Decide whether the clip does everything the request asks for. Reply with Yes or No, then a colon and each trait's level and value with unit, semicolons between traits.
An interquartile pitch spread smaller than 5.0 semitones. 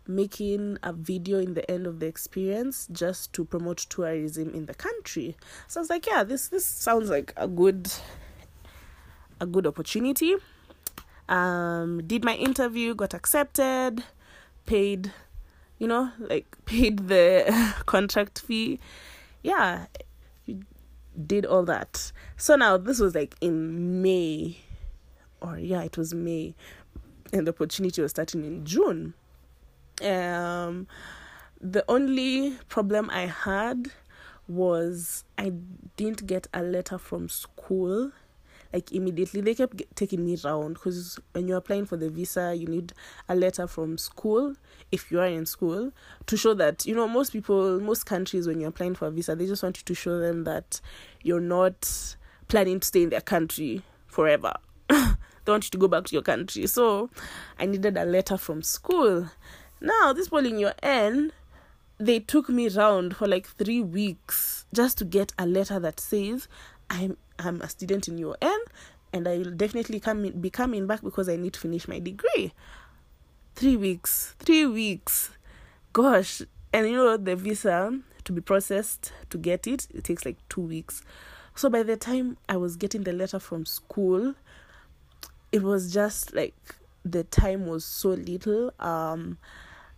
Yes: average, 4.4 semitones